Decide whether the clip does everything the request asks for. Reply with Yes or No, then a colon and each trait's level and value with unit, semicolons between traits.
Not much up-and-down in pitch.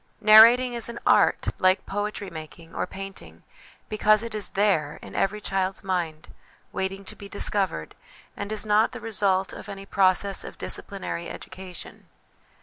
Yes: narrow, 2.2 semitones